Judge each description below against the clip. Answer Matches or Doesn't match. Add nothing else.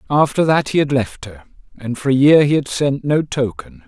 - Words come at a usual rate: Doesn't match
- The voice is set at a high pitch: Doesn't match